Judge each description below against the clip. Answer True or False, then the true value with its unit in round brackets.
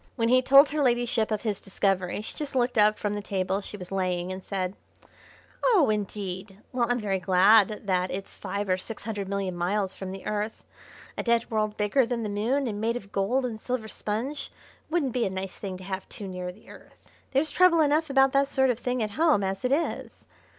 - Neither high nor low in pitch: False (210 Hz)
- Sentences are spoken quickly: True (220 wpm)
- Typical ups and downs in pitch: True (4.5 semitones)